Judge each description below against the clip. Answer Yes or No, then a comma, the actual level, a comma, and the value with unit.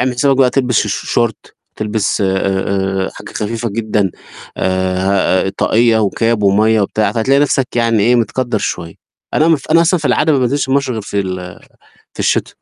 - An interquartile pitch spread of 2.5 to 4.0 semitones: No, average, 4.6 semitones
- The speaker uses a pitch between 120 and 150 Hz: No, low, 110 Hz